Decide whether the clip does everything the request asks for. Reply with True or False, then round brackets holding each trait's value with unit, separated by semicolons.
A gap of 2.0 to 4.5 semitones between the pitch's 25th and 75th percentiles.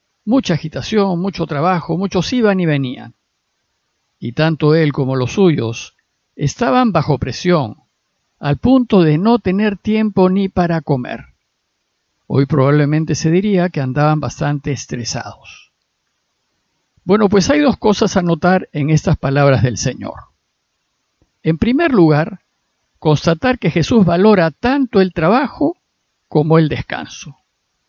False (5.6 semitones)